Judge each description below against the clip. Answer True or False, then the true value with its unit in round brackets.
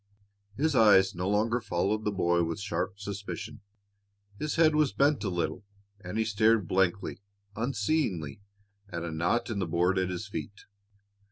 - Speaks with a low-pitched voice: True (100 Hz)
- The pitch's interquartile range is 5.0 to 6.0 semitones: False (4.1 semitones)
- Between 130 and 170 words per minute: True (160 wpm)